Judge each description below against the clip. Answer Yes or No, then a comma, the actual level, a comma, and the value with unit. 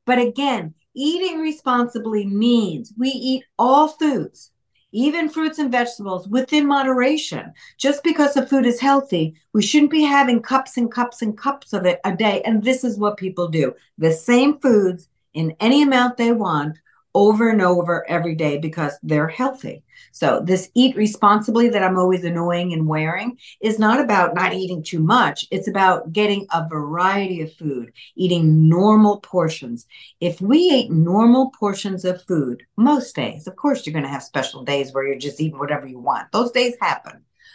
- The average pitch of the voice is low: No, high, 210 Hz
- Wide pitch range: Yes, wide, 7.3 semitones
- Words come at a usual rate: Yes, average, 175 wpm